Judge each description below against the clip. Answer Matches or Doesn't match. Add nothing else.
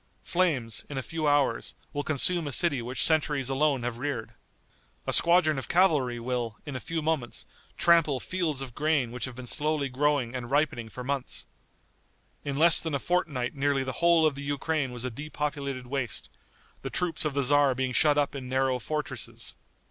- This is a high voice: Doesn't match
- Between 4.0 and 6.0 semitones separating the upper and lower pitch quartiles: Doesn't match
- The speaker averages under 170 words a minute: Doesn't match